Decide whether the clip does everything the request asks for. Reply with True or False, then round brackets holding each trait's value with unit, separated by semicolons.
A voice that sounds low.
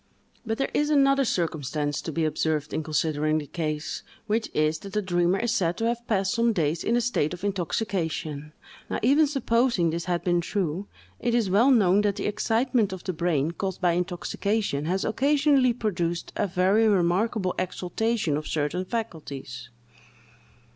False (185 Hz)